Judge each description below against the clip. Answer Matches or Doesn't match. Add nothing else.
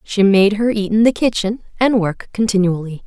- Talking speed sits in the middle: Matches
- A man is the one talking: Doesn't match